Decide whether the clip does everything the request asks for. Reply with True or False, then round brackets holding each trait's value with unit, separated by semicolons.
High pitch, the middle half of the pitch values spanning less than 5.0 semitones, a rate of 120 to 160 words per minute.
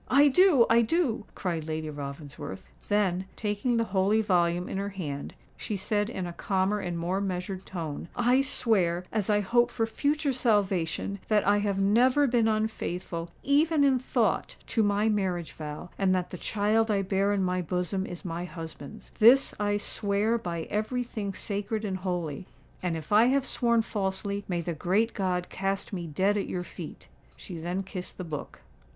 False (200 Hz; 3.7 semitones; 180 wpm)